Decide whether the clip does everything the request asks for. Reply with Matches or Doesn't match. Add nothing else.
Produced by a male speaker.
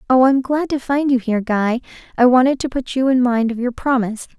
Doesn't match